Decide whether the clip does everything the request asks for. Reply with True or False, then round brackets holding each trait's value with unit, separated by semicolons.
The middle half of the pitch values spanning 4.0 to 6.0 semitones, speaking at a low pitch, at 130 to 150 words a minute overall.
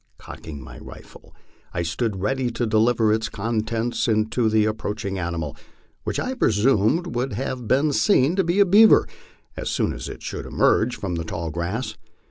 False (4.8 semitones; 110 Hz; 165 wpm)